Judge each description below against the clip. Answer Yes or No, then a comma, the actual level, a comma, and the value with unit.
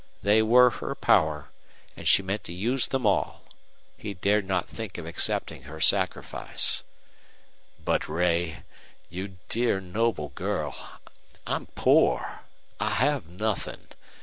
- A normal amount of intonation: Yes, average, 4.1 semitones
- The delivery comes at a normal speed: No, slow, 125 wpm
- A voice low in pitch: Yes, low, 100 Hz